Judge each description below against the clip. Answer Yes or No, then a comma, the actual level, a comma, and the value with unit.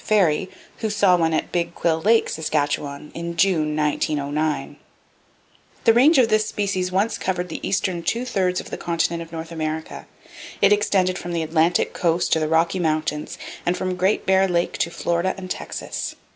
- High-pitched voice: No, medium, 175 Hz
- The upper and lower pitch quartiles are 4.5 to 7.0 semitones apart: No, average, 3.1 semitones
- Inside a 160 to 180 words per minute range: Yes, average, 175 wpm